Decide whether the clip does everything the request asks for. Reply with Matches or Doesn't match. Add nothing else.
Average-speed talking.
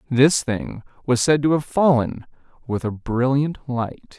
Matches